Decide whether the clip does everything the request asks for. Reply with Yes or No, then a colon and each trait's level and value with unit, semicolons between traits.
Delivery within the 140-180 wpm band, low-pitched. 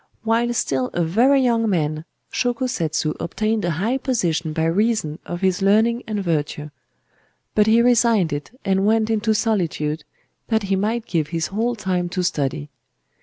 No: average, 165 wpm; high, 195 Hz